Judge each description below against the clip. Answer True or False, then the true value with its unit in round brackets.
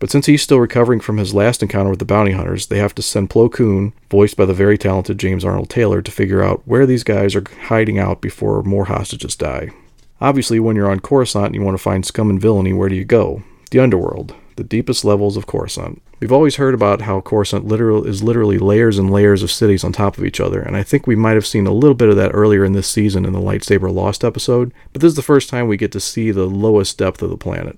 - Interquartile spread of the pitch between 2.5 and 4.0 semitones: True (2.9 semitones)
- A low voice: True (105 Hz)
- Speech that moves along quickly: True (260 wpm)